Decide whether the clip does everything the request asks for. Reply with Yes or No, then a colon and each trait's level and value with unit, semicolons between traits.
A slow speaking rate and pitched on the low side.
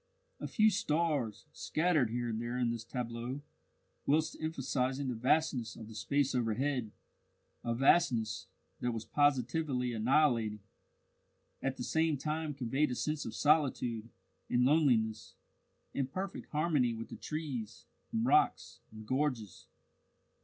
Yes: slow, 130 wpm; low, 130 Hz